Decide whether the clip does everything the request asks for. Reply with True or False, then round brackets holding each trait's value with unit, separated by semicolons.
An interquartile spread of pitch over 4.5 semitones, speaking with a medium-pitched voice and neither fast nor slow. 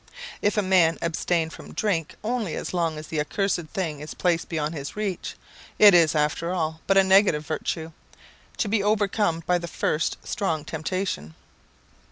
False (3.7 semitones; 170 Hz; 170 wpm)